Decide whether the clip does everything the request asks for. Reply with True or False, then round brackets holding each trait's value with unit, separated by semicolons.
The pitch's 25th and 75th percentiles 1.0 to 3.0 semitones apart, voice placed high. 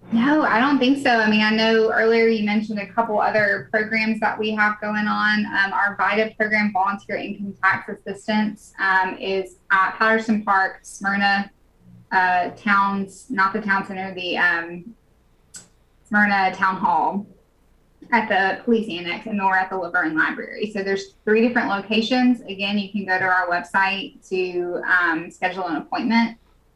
True (2.5 semitones; 200 Hz)